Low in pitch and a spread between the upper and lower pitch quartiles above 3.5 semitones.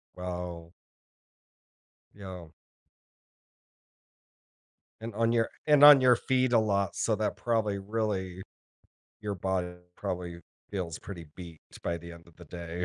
Yes: very low, 95 Hz; average, 4.1 semitones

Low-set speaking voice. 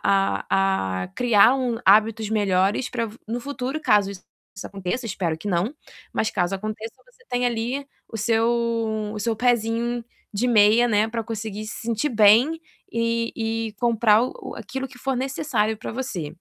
No: high, 225 Hz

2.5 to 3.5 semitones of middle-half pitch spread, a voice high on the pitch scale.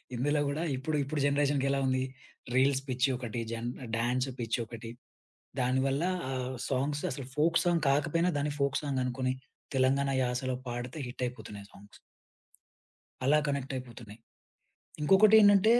No: average, 2.8 semitones; low, 135 Hz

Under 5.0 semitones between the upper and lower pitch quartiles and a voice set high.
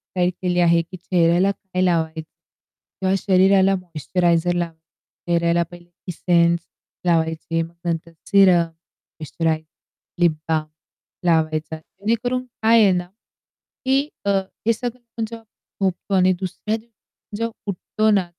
No: average, 2.9 semitones; medium, 180 Hz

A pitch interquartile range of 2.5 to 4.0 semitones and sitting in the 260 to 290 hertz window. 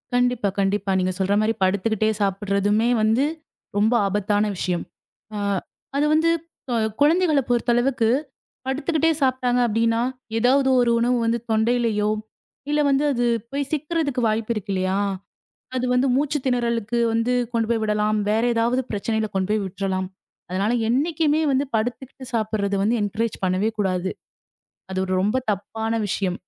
No: average, 3.7 semitones; high, 225 Hz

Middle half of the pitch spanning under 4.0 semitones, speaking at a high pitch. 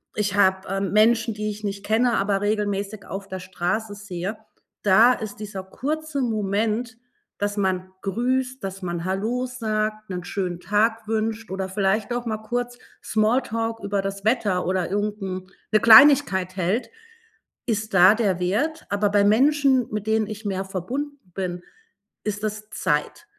Yes: average, 2.7 semitones; high, 210 Hz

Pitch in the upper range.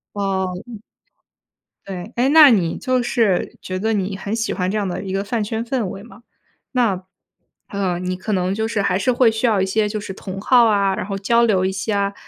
Yes: high, 200 Hz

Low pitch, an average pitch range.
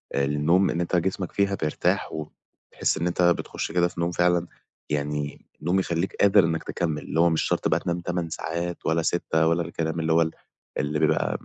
No: very low, 85 Hz; narrow, 1.7 semitones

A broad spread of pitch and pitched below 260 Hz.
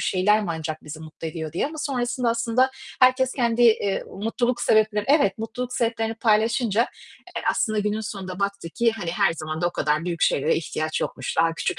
Yes: wide, 5.9 semitones; high, 210 Hz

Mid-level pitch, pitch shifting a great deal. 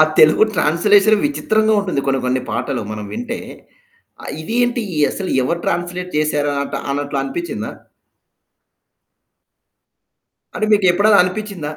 Yes: medium, 175 Hz; wide, 6.7 semitones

